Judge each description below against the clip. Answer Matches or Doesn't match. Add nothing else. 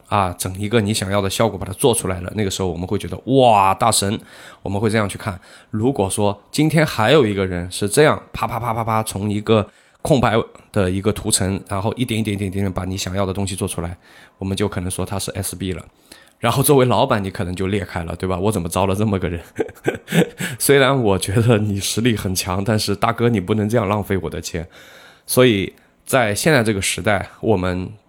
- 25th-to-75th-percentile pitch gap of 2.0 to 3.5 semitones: Matches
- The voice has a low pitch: Matches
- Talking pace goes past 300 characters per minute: Matches